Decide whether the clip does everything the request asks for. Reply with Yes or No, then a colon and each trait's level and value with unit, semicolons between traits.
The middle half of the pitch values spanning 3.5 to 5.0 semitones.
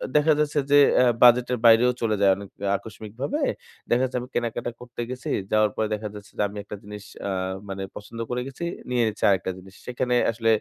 No: average, 3.1 semitones